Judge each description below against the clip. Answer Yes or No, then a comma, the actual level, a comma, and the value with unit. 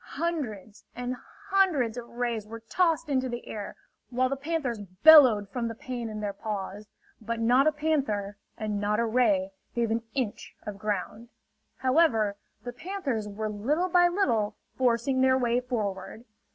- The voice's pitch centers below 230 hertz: No, high, 235 Hz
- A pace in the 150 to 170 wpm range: Yes, average, 160 wpm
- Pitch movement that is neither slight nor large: Yes, average, 4.3 semitones